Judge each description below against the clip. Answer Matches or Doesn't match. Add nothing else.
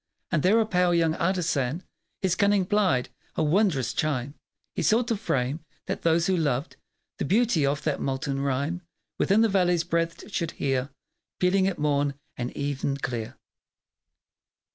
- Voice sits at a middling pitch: Matches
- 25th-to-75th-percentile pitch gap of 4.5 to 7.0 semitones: Matches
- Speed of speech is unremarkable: Matches